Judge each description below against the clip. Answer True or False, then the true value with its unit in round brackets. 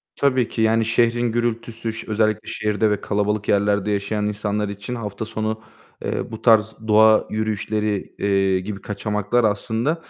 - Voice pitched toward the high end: False (110 Hz)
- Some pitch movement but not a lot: False (1.5 semitones)